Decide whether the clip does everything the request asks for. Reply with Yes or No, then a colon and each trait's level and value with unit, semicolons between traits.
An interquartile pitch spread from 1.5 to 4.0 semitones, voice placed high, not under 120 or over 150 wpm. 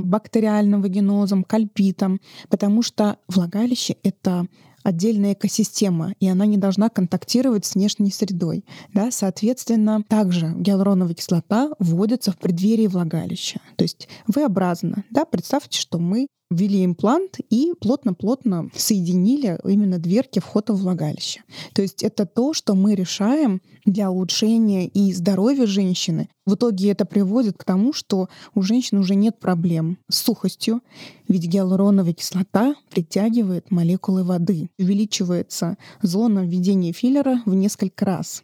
Yes: average, 2.9 semitones; high, 200 Hz; average, 130 wpm